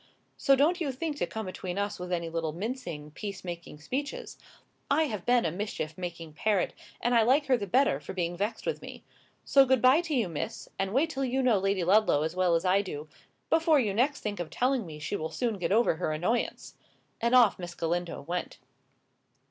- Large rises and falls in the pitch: Yes, wide, 6.6 semitones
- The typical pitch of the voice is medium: No, high, 205 Hz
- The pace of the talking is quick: Yes, fast, 215 wpm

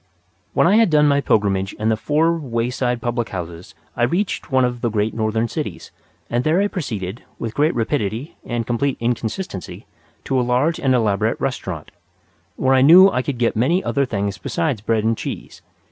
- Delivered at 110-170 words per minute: No, average, 185 wpm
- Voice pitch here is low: Yes, low, 120 Hz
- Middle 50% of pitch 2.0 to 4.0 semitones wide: No, average, 4.6 semitones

